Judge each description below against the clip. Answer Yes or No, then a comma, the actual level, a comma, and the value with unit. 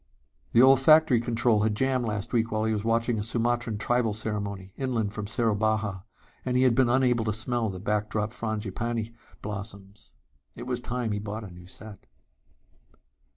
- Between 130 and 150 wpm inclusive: No, average, 165 wpm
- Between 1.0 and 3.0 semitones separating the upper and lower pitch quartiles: Yes, narrow, 2.5 semitones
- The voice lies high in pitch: No, low, 110 Hz